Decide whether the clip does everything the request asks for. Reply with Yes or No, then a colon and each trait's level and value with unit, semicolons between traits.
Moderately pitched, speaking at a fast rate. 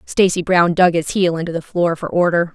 Yes: medium, 175 Hz; fast, 235 wpm